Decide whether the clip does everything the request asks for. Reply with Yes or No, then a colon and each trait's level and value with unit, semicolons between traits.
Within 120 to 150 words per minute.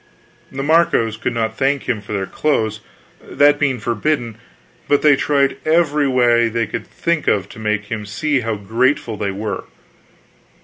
No: average, 165 wpm